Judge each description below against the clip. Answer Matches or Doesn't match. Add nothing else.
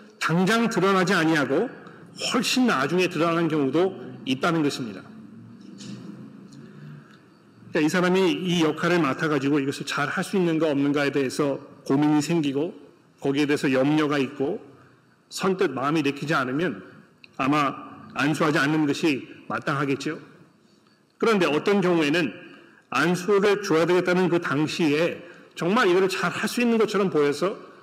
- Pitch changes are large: Doesn't match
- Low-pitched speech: Doesn't match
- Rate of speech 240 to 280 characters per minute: Doesn't match